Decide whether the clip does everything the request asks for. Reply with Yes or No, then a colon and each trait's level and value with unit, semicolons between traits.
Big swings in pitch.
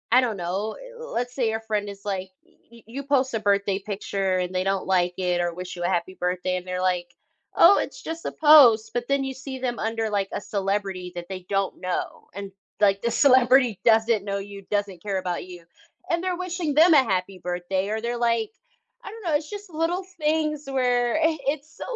Yes: wide, 6.0 semitones